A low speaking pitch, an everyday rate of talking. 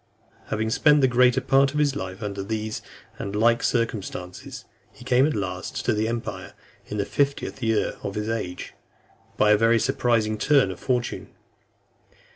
Yes: low, 110 Hz; average, 175 wpm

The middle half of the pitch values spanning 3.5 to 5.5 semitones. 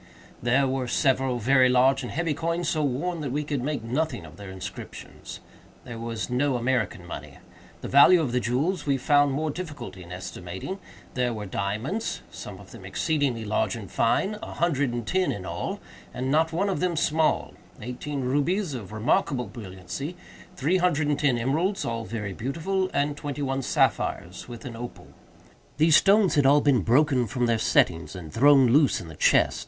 Yes: average, 4.8 semitones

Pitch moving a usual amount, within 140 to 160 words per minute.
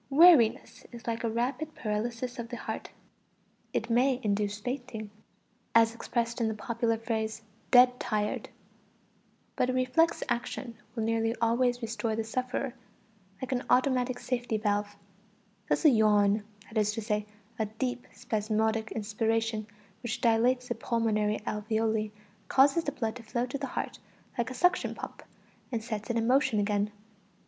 No: narrow, 2.3 semitones; average, 155 wpm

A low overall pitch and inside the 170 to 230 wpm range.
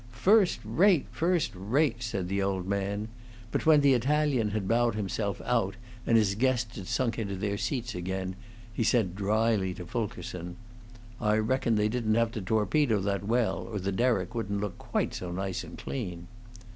Yes: low, 110 Hz; average, 175 wpm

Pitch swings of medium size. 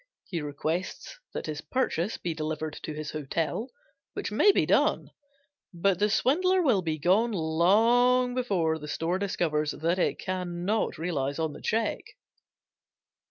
No: wide, 5.9 semitones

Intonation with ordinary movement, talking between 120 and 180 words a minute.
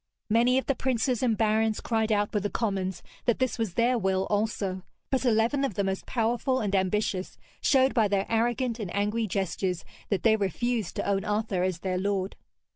No: average, 3.4 semitones; average, 195 wpm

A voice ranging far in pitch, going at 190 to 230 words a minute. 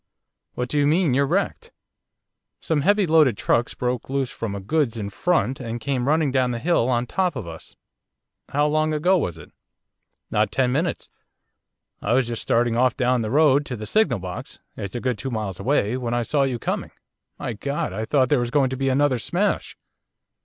No: average, 3.9 semitones; fast, 205 wpm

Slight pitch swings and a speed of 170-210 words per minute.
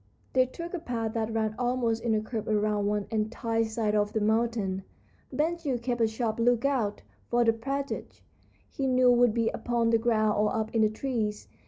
Yes: narrow, 2.2 semitones; average, 195 wpm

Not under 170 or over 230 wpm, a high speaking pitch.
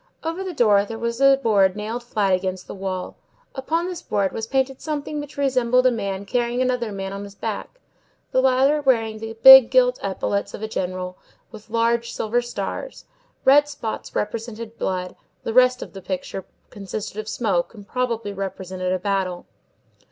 Yes: average, 175 wpm; high, 225 Hz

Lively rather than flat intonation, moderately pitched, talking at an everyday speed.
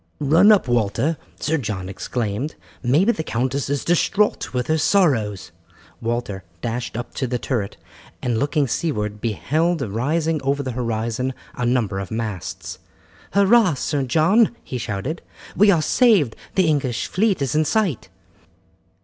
No: wide, 5.8 semitones; low, 130 Hz; average, 145 wpm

